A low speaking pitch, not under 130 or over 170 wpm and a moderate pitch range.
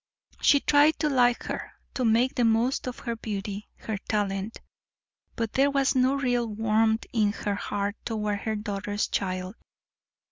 No: high, 225 Hz; average, 155 wpm; average, 3.4 semitones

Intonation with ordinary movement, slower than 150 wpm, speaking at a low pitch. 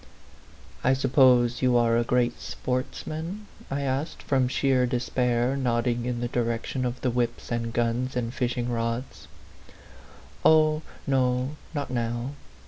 No: narrow, 1.8 semitones; average, 140 wpm; low, 125 Hz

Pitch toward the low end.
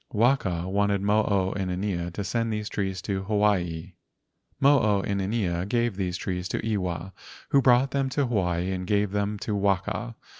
Yes: low, 100 Hz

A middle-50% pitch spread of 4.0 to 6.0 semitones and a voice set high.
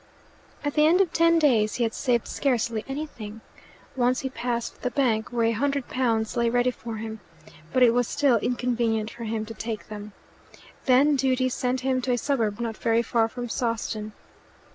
No: narrow, 2.6 semitones; high, 240 Hz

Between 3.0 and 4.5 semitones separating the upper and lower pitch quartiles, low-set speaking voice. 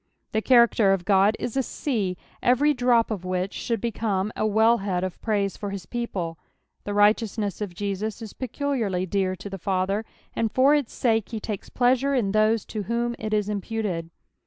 No: average, 3.3 semitones; high, 215 Hz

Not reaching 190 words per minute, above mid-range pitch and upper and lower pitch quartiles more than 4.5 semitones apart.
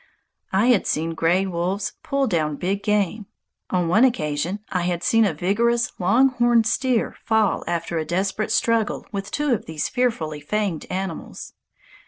Yes: average, 160 wpm; high, 195 Hz; average, 4.9 semitones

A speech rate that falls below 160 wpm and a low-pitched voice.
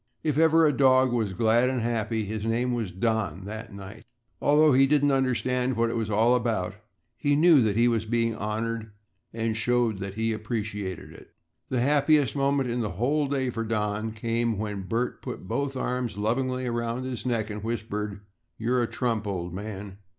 No: average, 185 wpm; low, 115 Hz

